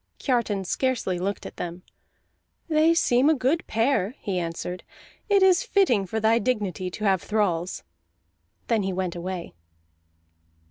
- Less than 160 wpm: Yes, average, 140 wpm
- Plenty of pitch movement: Yes, wide, 6.0 semitones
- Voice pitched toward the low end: No, high, 210 Hz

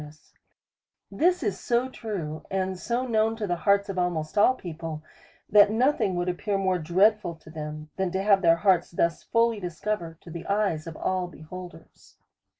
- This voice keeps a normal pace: No, fast, 210 wpm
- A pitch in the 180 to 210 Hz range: Yes, medium, 185 Hz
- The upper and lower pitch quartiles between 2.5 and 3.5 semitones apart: No, average, 4.1 semitones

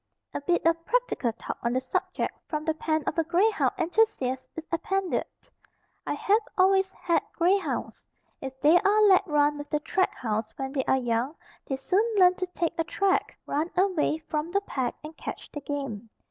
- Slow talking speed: No, average, 195 wpm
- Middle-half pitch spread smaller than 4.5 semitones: No, wide, 5.6 semitones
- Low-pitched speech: No, very high, 325 Hz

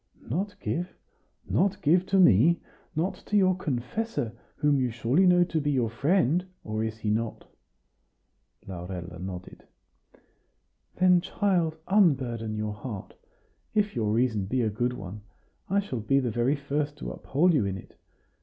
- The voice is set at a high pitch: No, low, 135 Hz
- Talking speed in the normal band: Yes, average, 155 wpm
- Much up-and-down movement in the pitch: Yes, wide, 8.1 semitones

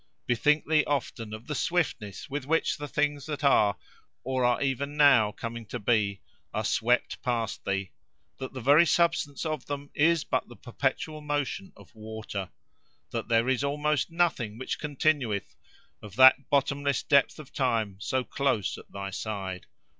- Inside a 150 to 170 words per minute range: Yes, average, 160 wpm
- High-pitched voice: No, low, 130 Hz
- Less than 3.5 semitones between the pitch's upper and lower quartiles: No, average, 5.0 semitones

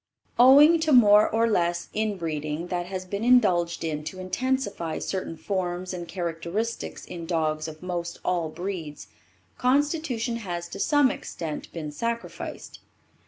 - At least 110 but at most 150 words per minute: Yes, slow, 135 wpm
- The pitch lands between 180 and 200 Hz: Yes, medium, 185 Hz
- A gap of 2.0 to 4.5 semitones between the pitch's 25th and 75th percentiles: No, wide, 5.4 semitones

